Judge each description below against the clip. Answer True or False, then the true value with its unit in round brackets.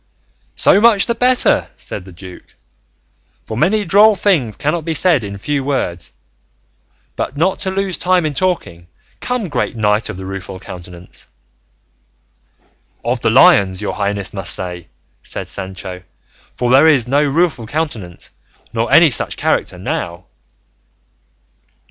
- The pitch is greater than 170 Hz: False (125 Hz)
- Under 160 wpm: True (140 wpm)